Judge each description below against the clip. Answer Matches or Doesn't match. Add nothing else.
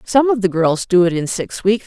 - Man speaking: Doesn't match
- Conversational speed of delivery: Doesn't match